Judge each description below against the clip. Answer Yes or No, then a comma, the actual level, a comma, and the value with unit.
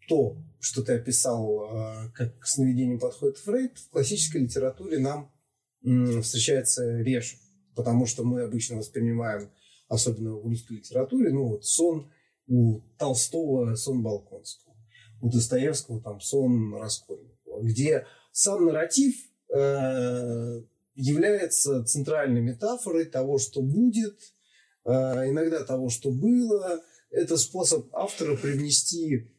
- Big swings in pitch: No, average, 5.0 semitones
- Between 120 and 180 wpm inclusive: No, slow, 110 wpm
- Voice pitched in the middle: No, low, 130 Hz